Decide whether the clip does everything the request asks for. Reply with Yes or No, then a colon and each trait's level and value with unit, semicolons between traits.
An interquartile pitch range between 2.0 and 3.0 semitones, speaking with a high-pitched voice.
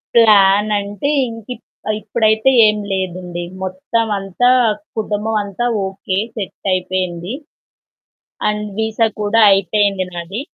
Yes: average, 2.7 semitones; high, 205 Hz